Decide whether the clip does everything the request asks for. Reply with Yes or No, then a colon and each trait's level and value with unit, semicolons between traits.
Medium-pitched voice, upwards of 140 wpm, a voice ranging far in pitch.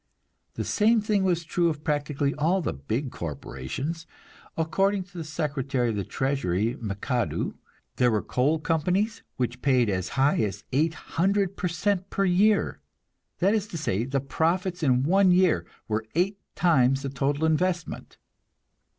Yes: medium, 155 Hz; average, 150 wpm; wide, 6.2 semitones